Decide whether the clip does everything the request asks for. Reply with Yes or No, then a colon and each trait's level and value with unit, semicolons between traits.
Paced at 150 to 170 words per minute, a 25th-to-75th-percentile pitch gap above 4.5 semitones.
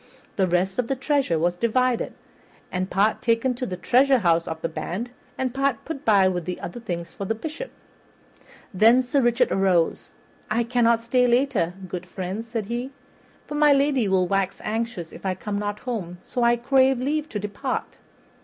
No: average, 180 wpm; average, 5.2 semitones